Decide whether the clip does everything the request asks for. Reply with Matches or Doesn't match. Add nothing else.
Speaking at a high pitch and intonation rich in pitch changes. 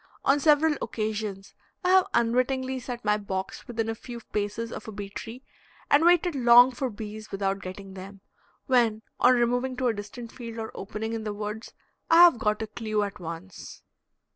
Doesn't match